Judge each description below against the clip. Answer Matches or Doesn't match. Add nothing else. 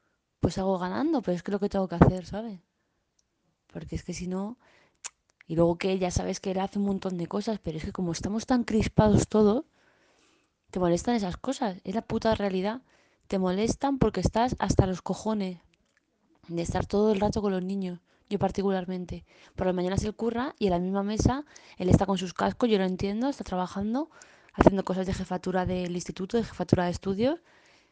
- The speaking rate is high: Matches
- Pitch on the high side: Matches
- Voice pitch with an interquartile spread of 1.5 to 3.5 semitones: Matches